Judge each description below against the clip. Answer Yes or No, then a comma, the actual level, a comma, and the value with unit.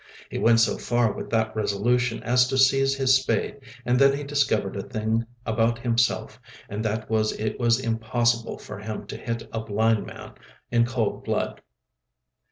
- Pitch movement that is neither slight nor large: No, narrow, 2.1 semitones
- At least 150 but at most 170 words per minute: No, average, 180 wpm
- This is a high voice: No, low, 115 Hz